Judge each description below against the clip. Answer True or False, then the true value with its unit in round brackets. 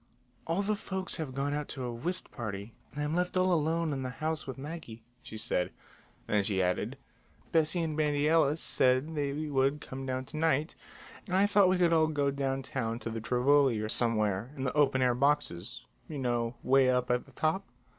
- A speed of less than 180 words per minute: False (205 wpm)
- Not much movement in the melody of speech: False (4.2 semitones)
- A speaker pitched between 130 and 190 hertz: True (140 Hz)